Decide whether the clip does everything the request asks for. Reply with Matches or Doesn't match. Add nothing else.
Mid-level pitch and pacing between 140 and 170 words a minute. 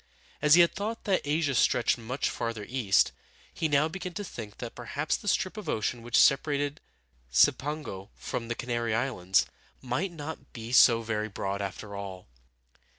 Doesn't match